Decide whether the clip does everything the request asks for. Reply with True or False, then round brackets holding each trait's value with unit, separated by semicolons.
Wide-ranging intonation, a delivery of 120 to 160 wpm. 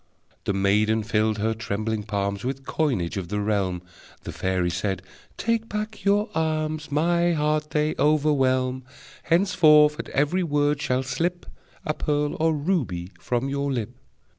True (6.5 semitones; 145 wpm)